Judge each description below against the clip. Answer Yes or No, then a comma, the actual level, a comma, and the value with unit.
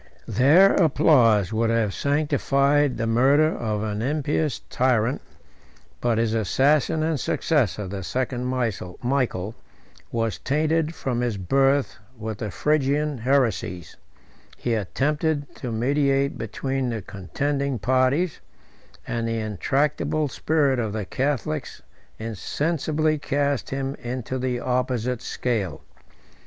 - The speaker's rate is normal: No, slow, 115 wpm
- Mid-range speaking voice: No, low, 130 Hz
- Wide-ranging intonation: No, average, 4.1 semitones